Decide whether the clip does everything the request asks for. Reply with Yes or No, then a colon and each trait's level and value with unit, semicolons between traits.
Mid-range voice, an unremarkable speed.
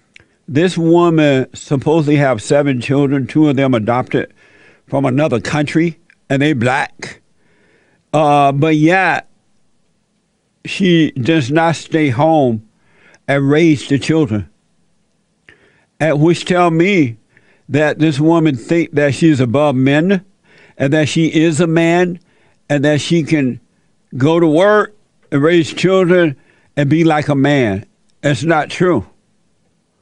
No: medium, 155 Hz; slow, 130 wpm